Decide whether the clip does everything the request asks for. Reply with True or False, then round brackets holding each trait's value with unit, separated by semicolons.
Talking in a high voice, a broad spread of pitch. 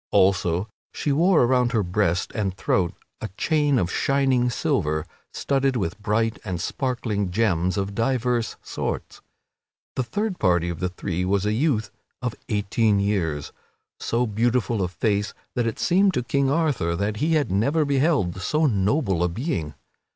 False (110 Hz; 6.2 semitones)